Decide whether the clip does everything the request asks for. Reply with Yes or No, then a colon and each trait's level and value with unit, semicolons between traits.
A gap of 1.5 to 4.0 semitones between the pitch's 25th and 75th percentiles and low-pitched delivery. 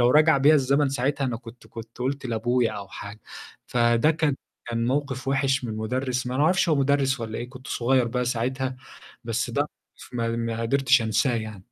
Yes: average, 2.9 semitones; low, 125 Hz